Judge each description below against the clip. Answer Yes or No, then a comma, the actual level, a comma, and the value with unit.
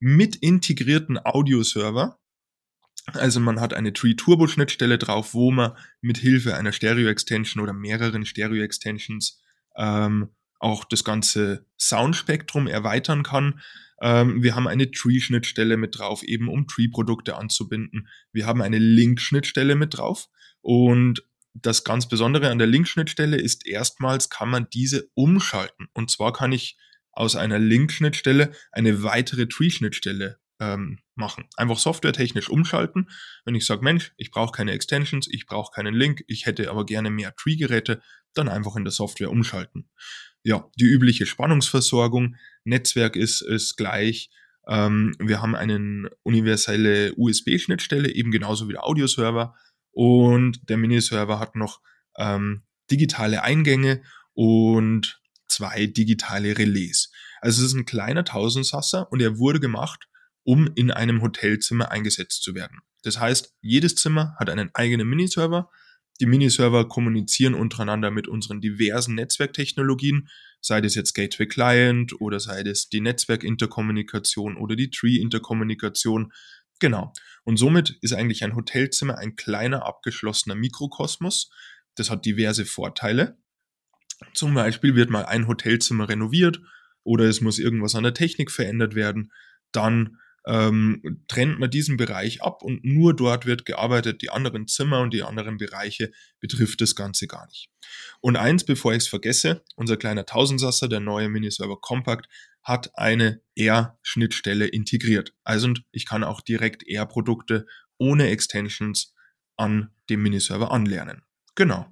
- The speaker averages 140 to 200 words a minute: Yes, average, 145 wpm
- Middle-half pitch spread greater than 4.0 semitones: No, average, 3.3 semitones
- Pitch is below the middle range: Yes, low, 115 Hz